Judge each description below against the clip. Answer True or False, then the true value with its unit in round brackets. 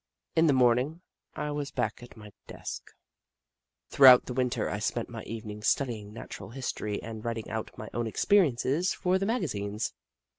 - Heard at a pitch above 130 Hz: False (125 Hz)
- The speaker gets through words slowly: False (160 wpm)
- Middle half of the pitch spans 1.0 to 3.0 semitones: False (4.9 semitones)